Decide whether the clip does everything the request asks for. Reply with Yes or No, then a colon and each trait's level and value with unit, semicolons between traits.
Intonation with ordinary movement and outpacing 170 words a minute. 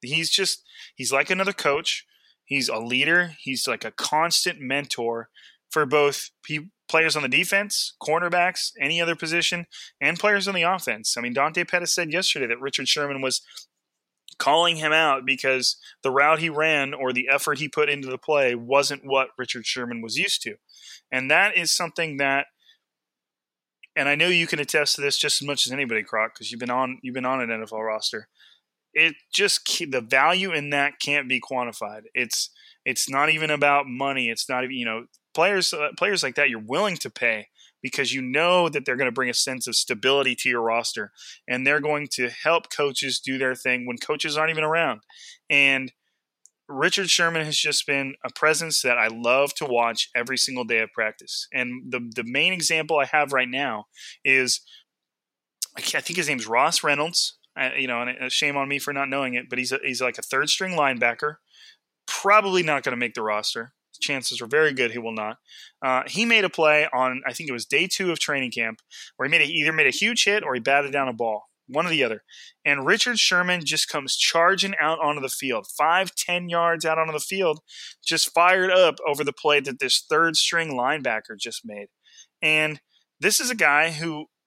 Yes: average, 4.1 semitones; fast, 205 wpm